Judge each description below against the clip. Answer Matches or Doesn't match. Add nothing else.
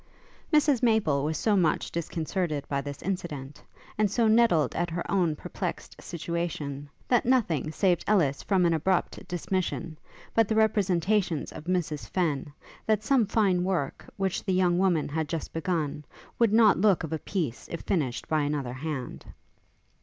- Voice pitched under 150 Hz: Doesn't match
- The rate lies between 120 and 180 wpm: Matches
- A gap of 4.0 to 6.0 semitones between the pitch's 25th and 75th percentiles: Matches